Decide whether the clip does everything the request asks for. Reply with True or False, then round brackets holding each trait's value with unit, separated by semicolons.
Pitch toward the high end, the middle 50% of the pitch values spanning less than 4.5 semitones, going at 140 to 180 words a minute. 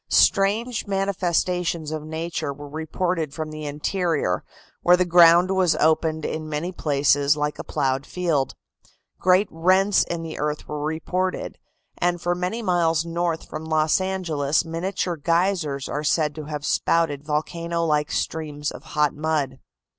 False (160 Hz; 3.0 semitones; 145 wpm)